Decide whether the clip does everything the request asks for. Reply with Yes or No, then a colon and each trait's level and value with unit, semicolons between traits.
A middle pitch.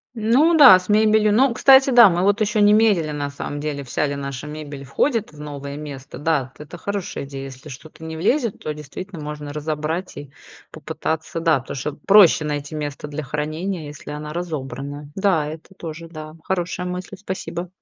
Yes: medium, 155 Hz